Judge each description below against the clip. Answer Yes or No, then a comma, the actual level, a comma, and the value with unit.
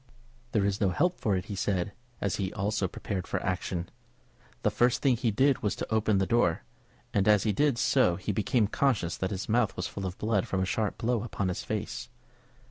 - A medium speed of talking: No, fast, 215 wpm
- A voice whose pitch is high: No, low, 105 Hz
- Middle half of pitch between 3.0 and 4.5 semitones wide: Yes, average, 3.4 semitones